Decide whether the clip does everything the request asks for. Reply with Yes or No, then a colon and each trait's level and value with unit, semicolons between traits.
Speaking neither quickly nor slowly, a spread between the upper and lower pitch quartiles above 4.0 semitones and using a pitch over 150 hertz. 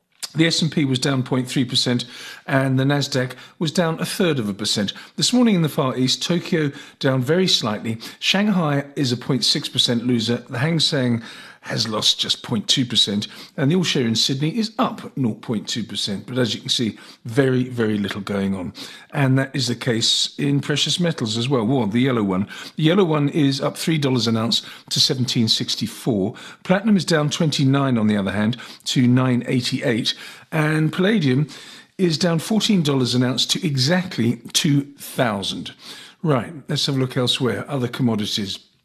No: average, 175 wpm; average, 4.8 semitones; low, 135 Hz